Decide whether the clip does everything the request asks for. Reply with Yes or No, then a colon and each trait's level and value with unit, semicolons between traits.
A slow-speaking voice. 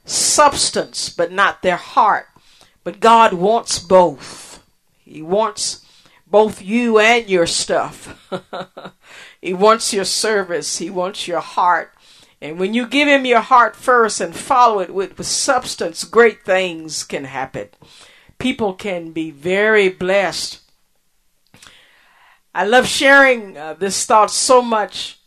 Yes: slow, 130 wpm